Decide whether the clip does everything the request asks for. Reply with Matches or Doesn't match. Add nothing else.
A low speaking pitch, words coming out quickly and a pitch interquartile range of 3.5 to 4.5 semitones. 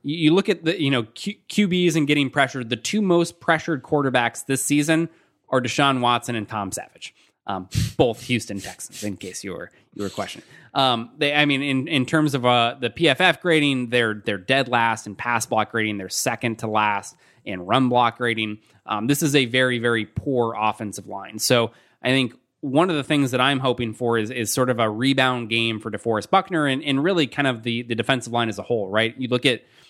Matches